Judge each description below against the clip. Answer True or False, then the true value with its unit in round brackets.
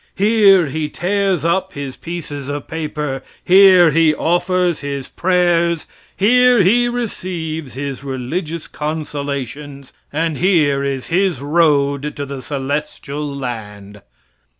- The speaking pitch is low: False (155 Hz)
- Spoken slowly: True (120 wpm)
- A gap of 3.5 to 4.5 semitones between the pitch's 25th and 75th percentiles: True (4.2 semitones)